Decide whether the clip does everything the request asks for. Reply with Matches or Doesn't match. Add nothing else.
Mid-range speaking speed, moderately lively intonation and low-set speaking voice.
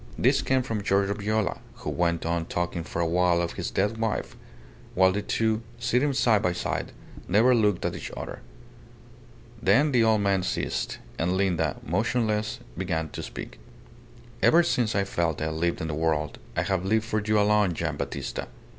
Matches